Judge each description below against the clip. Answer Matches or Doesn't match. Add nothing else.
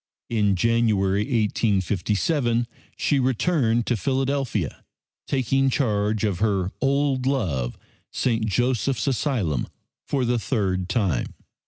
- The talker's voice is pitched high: Doesn't match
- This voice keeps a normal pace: Doesn't match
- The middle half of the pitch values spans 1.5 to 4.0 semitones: Doesn't match